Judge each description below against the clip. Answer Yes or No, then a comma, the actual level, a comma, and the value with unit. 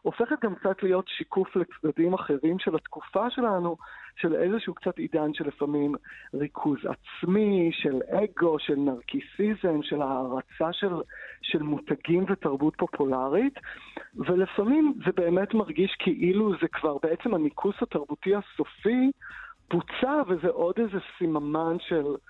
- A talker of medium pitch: Yes, medium, 180 Hz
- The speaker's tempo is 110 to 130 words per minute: Yes, average, 125 wpm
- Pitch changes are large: No, average, 4.7 semitones